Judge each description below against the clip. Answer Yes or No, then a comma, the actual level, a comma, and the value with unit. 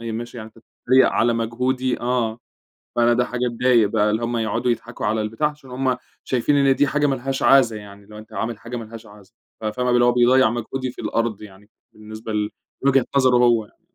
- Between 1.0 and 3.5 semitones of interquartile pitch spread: Yes, narrow, 2.5 semitones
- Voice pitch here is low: Yes, low, 120 Hz